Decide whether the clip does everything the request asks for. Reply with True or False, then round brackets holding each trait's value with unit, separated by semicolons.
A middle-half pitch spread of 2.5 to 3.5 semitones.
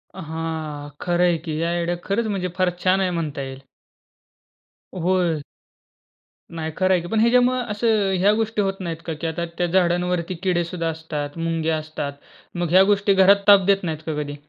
True (3.1 semitones)